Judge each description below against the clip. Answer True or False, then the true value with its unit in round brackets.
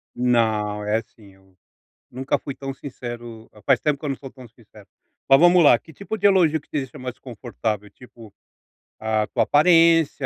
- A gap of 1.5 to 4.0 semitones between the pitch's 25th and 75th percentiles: False (4.9 semitones)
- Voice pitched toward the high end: False (125 Hz)